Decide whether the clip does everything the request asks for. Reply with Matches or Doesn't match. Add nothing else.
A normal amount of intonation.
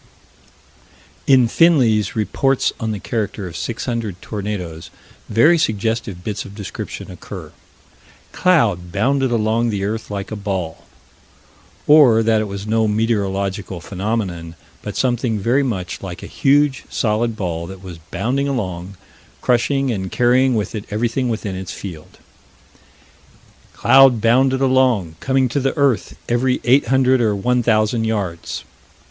Matches